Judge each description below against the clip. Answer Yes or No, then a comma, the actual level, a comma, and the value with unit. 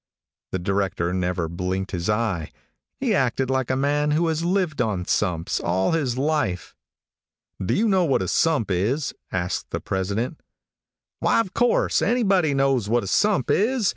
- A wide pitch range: Yes, wide, 9.0 semitones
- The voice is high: No, low, 125 Hz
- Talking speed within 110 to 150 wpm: No, average, 165 wpm